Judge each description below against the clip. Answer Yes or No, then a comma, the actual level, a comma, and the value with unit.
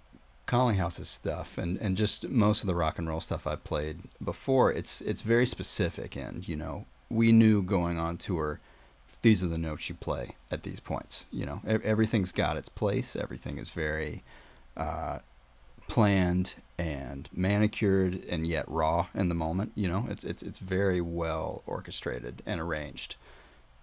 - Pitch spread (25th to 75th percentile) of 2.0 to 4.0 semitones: No, average, 4.9 semitones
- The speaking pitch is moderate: No, very low, 90 Hz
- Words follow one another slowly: No, average, 165 wpm